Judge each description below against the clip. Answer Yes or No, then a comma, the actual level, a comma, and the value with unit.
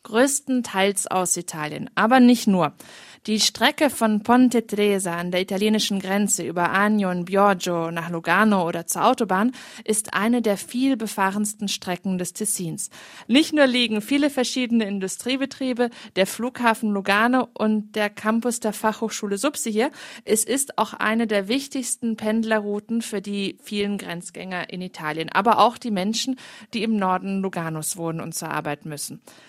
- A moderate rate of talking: Yes, average, 150 wpm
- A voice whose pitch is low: No, high, 215 Hz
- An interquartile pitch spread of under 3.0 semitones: No, average, 3.8 semitones